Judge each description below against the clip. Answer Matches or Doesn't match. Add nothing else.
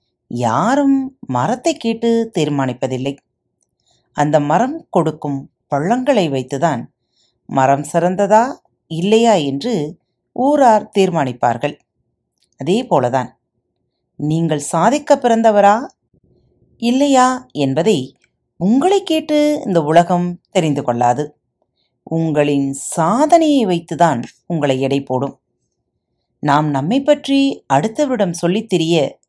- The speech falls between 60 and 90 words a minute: Matches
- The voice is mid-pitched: Matches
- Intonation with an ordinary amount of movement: Doesn't match